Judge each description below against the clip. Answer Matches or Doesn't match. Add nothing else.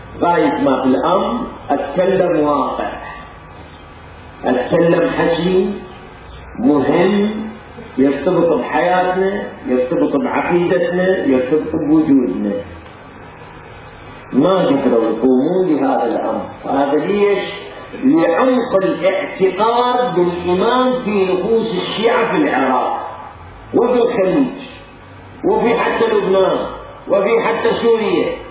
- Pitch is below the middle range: Doesn't match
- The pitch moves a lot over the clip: Matches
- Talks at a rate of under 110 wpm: Matches